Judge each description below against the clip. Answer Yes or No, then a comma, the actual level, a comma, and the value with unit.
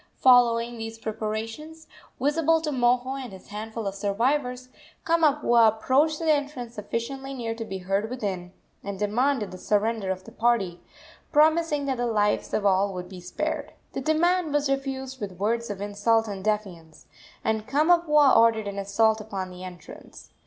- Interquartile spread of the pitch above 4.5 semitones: Yes, average, 5.0 semitones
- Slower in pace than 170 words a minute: Yes, average, 160 wpm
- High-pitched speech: Yes, high, 230 Hz